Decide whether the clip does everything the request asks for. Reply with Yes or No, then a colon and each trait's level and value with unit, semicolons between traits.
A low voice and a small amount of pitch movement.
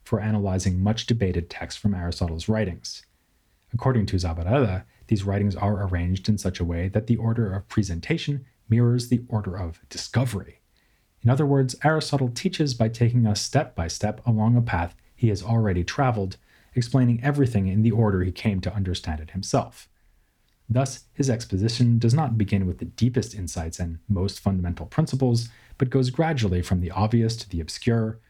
No: low, 110 Hz; average, 4.4 semitones